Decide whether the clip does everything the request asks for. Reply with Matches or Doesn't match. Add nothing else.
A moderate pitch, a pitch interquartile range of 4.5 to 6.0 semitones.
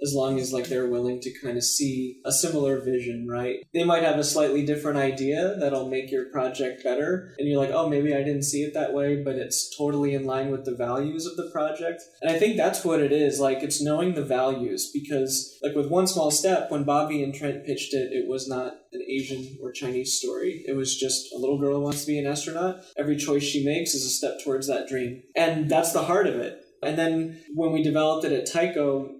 Doesn't match